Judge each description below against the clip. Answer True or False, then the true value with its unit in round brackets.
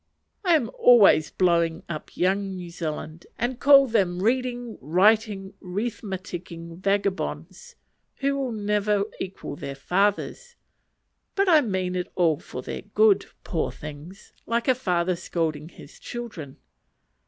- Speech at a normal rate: False (130 wpm)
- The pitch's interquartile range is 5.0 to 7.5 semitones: True (5.3 semitones)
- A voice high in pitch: True (195 Hz)